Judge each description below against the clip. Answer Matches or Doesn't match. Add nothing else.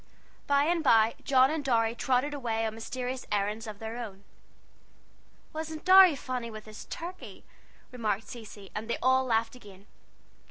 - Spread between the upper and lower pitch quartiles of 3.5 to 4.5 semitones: Matches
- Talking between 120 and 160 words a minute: Matches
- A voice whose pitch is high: Matches